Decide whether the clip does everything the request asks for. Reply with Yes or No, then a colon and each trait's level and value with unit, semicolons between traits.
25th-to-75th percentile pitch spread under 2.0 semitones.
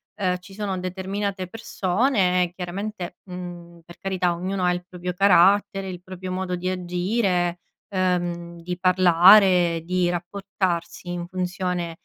Yes: narrow, 1.5 semitones